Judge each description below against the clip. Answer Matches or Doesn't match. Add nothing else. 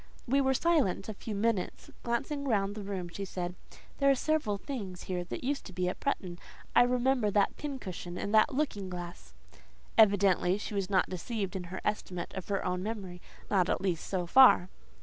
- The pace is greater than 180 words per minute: Matches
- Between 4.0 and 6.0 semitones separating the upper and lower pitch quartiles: Matches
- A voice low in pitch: Doesn't match